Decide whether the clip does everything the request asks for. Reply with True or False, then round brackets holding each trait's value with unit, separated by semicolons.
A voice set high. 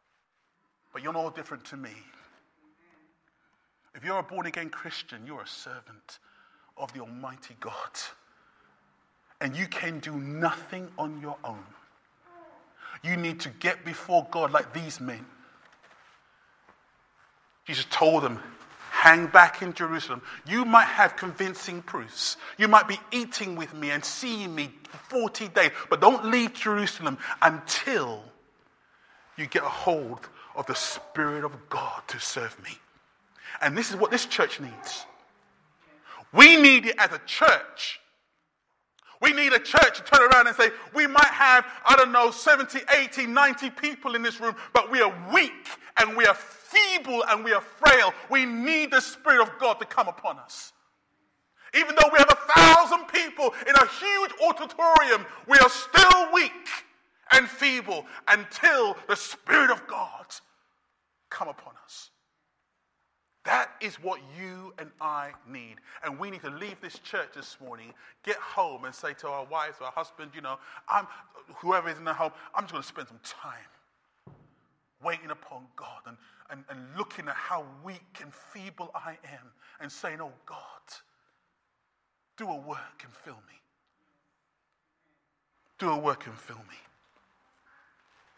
True (215 Hz)